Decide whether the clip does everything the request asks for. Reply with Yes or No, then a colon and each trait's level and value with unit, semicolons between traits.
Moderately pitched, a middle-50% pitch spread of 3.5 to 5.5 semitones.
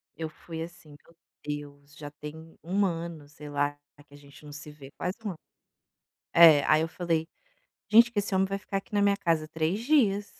Yes: medium, 160 Hz; average, 4.8 semitones